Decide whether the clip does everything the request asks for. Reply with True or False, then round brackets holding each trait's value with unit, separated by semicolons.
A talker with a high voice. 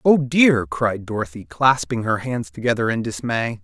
False (115 Hz)